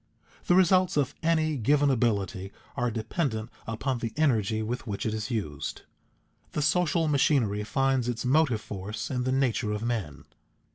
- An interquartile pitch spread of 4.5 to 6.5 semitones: Yes, average, 5.0 semitones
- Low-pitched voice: Yes, low, 120 Hz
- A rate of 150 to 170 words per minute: Yes, average, 160 wpm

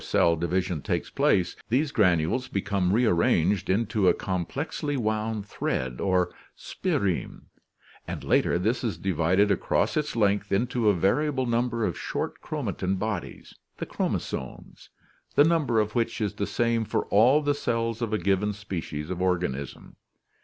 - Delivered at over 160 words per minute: No, average, 155 wpm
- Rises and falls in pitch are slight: No, average, 4.3 semitones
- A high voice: No, low, 105 Hz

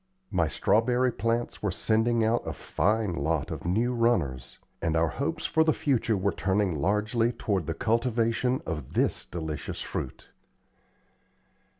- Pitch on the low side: Yes, low, 110 Hz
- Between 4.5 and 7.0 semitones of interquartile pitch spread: Yes, wide, 5.5 semitones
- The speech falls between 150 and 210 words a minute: No, average, 140 wpm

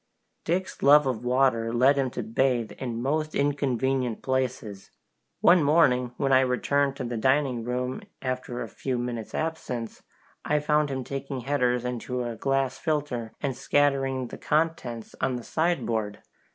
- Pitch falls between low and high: No, low, 130 Hz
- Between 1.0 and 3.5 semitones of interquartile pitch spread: Yes, narrow, 2.6 semitones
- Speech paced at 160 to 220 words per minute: No, average, 150 wpm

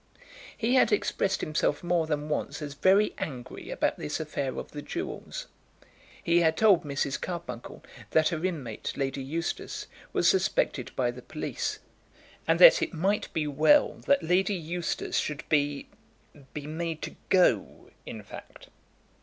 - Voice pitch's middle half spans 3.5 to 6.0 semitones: Yes, average, 4.4 semitones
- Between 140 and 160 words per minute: Yes, average, 150 wpm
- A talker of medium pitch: Yes, medium, 160 Hz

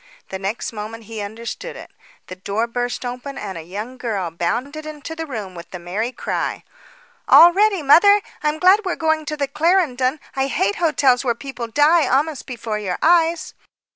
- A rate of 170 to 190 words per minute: Yes, average, 185 wpm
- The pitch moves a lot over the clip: Yes, wide, 6.4 semitones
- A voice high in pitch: Yes, very high, 260 Hz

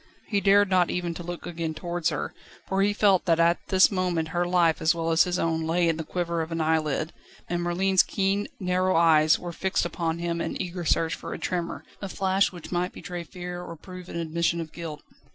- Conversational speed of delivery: No, fast, 225 wpm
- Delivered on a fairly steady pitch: Yes, narrow, 1.8 semitones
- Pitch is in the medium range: Yes, medium, 175 Hz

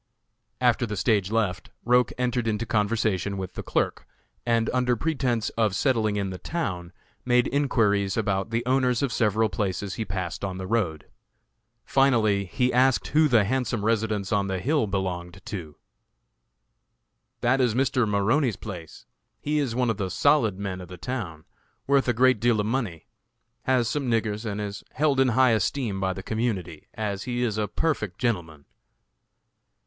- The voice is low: Yes, low, 110 Hz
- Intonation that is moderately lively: Yes, average, 4.3 semitones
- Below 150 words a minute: No, average, 165 wpm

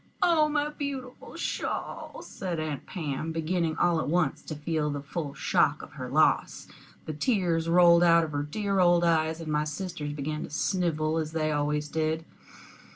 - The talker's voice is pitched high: No, medium, 160 Hz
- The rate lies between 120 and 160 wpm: No, average, 175 wpm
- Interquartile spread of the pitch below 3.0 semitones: Yes, narrow, 2.6 semitones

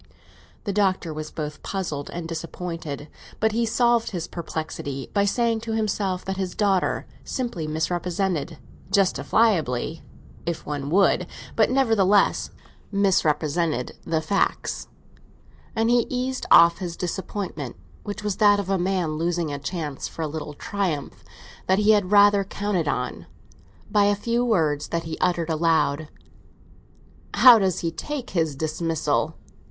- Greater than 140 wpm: No, slow, 135 wpm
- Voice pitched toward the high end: No, medium, 180 Hz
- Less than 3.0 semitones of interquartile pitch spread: No, average, 4.4 semitones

